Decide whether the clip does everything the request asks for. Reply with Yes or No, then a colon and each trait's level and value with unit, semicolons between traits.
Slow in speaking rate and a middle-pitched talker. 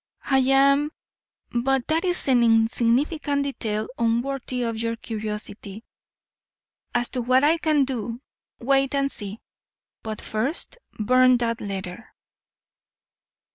No: slow, 115 wpm; high, 245 Hz